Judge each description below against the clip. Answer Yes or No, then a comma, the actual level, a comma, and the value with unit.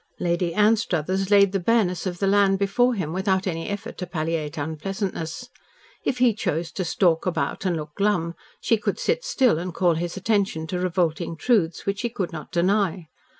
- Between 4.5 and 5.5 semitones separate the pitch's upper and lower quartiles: No, average, 3.4 semitones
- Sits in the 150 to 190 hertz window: Yes, medium, 185 Hz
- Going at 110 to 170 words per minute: No, average, 185 wpm